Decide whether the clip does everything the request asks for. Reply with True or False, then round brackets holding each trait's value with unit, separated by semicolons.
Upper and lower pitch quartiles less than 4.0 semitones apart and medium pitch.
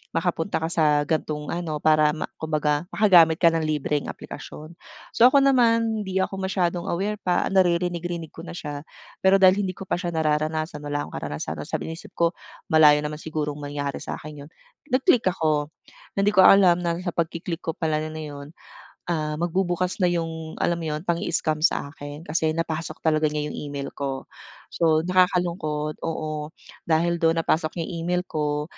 True (2.7 semitones; 160 Hz)